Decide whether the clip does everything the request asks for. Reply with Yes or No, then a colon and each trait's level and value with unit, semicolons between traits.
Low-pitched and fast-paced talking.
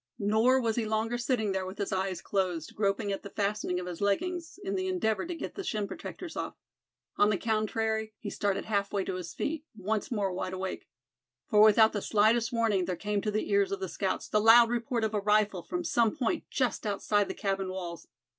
No: high, 215 Hz; fast, 220 wpm